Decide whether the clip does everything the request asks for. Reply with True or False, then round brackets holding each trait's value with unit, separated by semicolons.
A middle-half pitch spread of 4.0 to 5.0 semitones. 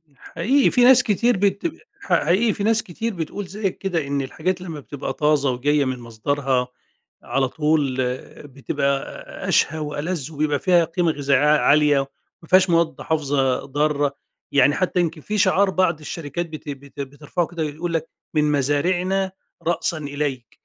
True (4.3 semitones)